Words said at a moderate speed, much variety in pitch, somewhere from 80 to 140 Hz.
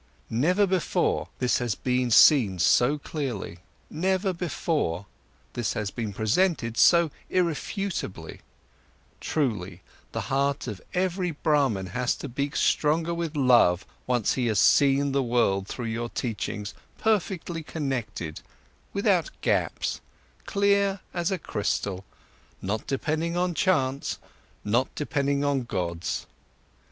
No: slow, 120 wpm; wide, 7.3 semitones; low, 135 Hz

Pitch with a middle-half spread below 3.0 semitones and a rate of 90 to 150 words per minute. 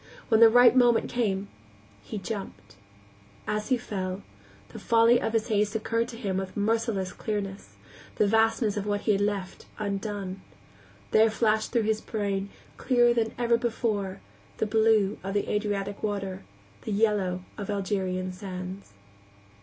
Yes: narrow, 2.4 semitones; average, 145 wpm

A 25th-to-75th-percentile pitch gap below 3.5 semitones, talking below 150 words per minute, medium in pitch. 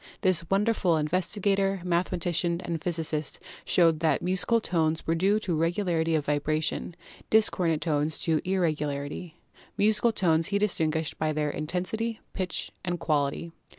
Yes: average, 3.1 semitones; slow, 135 wpm; medium, 170 Hz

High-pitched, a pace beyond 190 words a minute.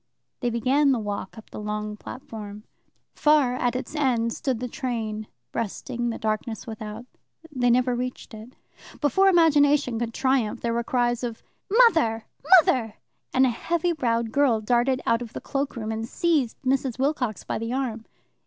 No: high, 240 Hz; average, 165 wpm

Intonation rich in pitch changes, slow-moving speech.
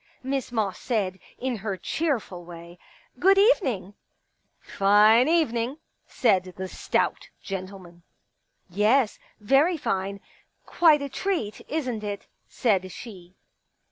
Yes: wide, 6.2 semitones; slow, 125 wpm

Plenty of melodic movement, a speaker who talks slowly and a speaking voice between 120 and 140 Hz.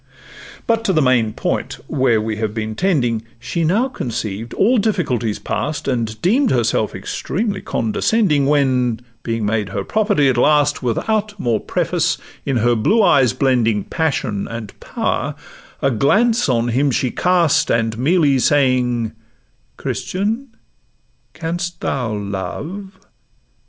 Yes: wide, 7.9 semitones; slow, 130 wpm; low, 135 Hz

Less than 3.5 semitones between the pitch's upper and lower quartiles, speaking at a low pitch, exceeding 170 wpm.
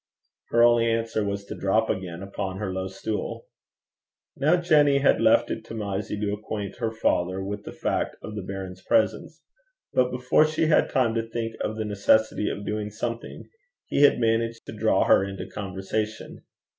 Yes: average, 2.9 semitones; low, 110 Hz; average, 180 wpm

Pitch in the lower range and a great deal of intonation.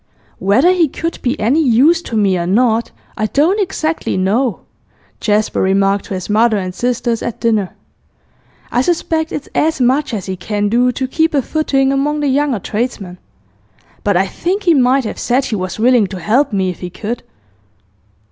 No: high, 240 Hz; wide, 5.8 semitones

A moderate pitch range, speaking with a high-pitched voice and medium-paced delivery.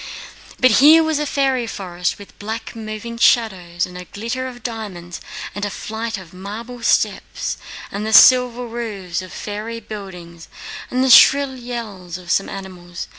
Yes: average, 4.5 semitones; high, 215 Hz; average, 160 wpm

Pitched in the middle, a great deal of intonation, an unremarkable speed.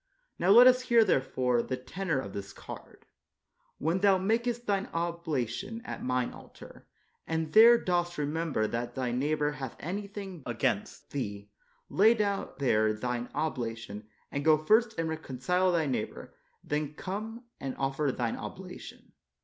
Yes: medium, 155 Hz; wide, 7.6 semitones; average, 155 wpm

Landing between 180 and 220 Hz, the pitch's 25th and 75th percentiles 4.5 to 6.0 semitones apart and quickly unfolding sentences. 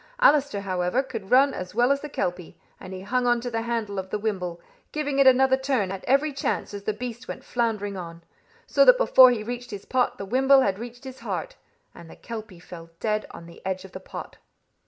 No: high, 230 Hz; wide, 5.4 semitones; fast, 225 wpm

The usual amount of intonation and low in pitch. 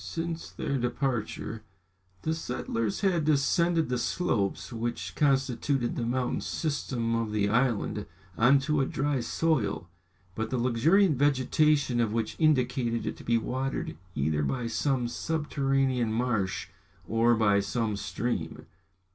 Yes: average, 3.8 semitones; low, 125 Hz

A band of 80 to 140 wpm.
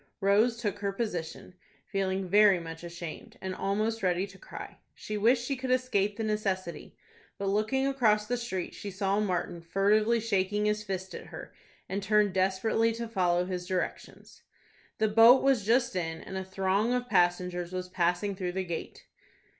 No: average, 170 wpm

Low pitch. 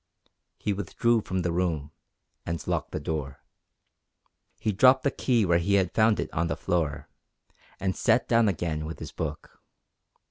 Yes: very low, 90 Hz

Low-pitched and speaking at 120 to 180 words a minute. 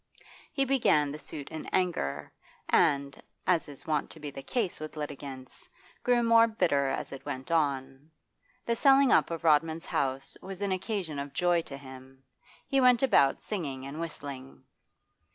No: medium, 155 Hz; average, 165 wpm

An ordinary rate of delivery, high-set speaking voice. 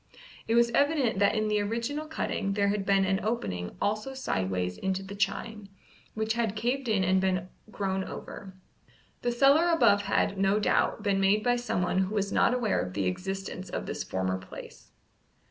Yes: average, 180 wpm; high, 205 Hz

